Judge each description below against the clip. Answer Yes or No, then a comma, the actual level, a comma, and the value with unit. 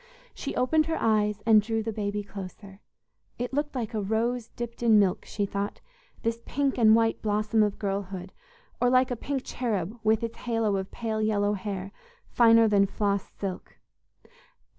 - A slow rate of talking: No, average, 170 wpm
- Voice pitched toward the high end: Yes, high, 215 Hz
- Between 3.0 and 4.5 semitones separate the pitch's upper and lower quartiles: No, narrow, 2.5 semitones